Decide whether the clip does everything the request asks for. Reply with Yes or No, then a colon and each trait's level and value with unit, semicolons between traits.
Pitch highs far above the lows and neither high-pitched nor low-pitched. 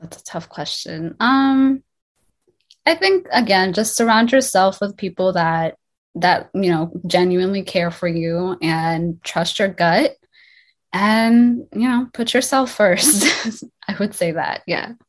No: wide, 5.9 semitones; high, 195 Hz